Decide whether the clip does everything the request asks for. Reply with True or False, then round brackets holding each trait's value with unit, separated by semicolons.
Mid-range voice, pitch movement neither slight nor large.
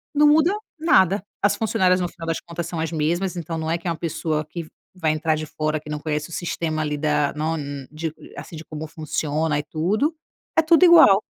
True (165 Hz; 3.2 semitones)